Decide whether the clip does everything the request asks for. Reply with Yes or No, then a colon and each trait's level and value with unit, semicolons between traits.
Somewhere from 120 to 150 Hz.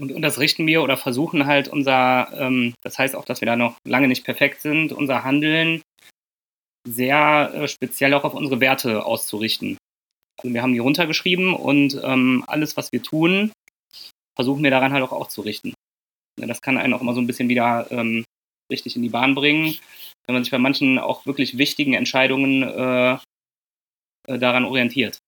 Yes: low, 130 Hz